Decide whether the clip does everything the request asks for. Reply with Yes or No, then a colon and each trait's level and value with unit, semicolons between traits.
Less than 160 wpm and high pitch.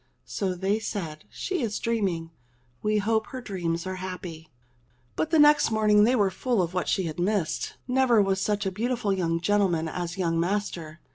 No: average, 180 wpm; high, 195 Hz